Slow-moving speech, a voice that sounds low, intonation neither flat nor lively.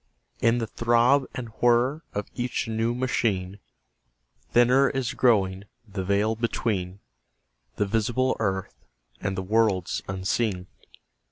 Yes: slow, 115 wpm; low, 115 Hz; average, 3.8 semitones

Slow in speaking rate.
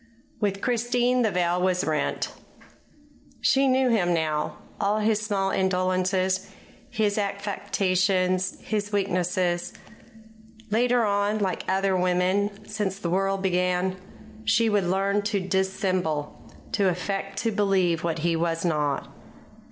Yes: slow, 125 wpm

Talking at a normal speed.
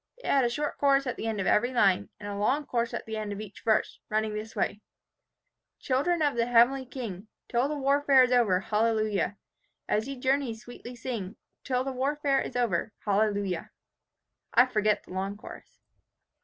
Yes: average, 185 wpm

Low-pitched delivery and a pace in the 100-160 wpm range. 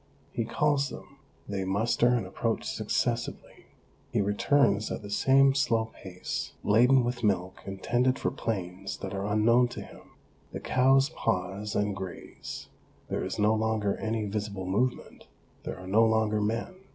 Yes: low, 110 Hz; average, 150 wpm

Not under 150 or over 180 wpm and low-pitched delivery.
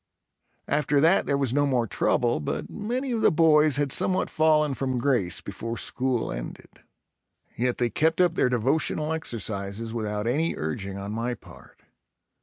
Yes: average, 160 wpm; low, 130 Hz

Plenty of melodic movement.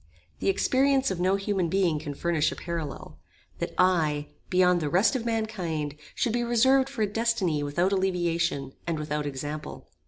Yes: wide, 6.2 semitones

